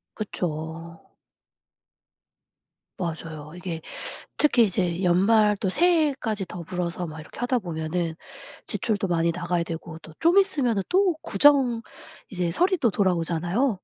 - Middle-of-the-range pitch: Yes, medium, 180 Hz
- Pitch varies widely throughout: Yes, wide, 6.1 semitones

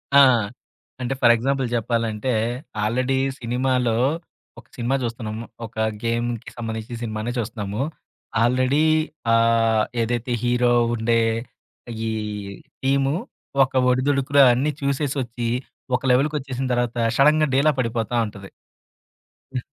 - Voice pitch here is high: No, low, 120 Hz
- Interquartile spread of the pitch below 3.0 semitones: Yes, narrow, 2.5 semitones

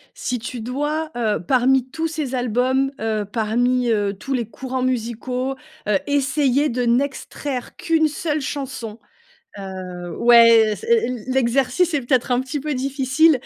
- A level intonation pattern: No, average, 3.1 semitones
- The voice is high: Yes, very high, 255 Hz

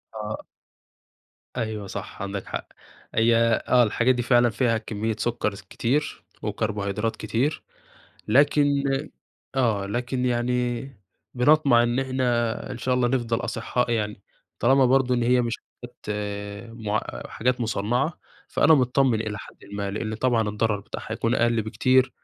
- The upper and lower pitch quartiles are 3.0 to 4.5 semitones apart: No, narrow, 2.6 semitones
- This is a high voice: No, low, 120 Hz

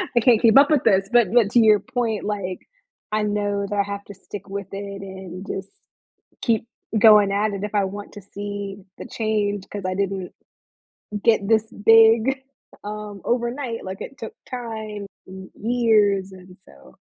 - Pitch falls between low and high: No, high, 205 Hz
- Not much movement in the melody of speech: Yes, narrow, 2.3 semitones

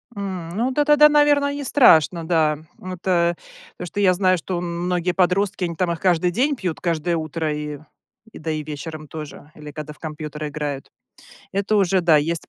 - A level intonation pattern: No, average, 3.8 semitones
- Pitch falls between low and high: Yes, medium, 170 Hz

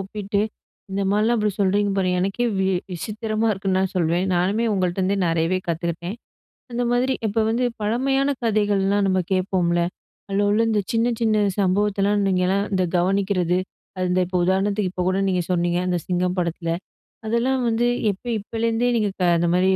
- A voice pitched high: Yes, high, 195 Hz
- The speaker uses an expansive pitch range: No, average, 2.9 semitones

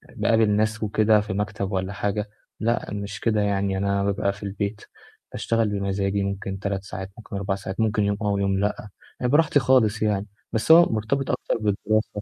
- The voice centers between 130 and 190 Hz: No, low, 105 Hz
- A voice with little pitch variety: Yes, narrow, 1.6 semitones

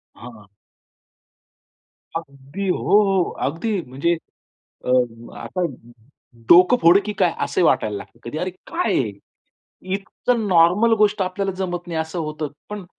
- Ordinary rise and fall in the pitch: Yes, average, 4.0 semitones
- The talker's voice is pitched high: No, medium, 180 Hz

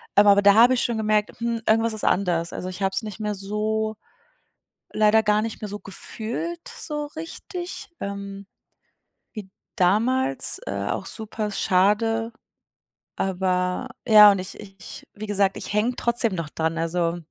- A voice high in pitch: Yes, high, 210 Hz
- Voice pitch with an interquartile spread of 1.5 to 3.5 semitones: Yes, average, 2.8 semitones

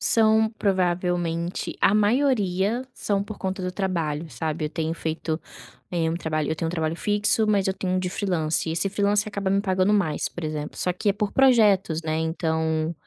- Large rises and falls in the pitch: No, average, 3.9 semitones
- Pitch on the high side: No, medium, 180 Hz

